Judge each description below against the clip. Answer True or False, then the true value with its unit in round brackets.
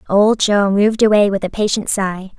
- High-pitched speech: True (200 Hz)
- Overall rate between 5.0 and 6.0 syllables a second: True (5.1 syllables/s)